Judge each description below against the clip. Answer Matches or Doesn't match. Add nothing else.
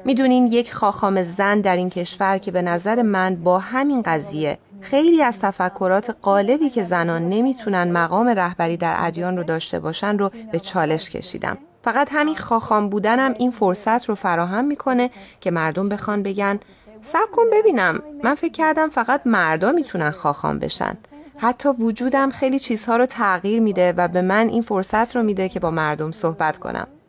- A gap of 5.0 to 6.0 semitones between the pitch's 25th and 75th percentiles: Matches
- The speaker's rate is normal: Doesn't match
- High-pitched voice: Matches